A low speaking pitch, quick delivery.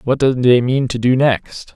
Yes: low, 125 Hz; fast, 240 wpm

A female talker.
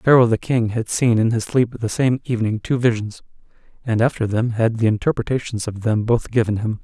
No: male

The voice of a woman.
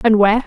Yes: female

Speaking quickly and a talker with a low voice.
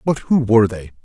Yes: fast, 230 wpm; low, 115 Hz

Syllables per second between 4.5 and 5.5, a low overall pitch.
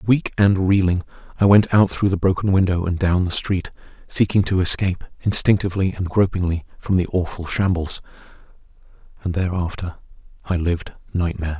No: 5.7 syllables/s; very low, 90 Hz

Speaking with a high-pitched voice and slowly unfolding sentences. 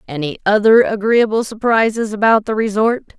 Yes: high, 215 Hz; slow, 130 wpm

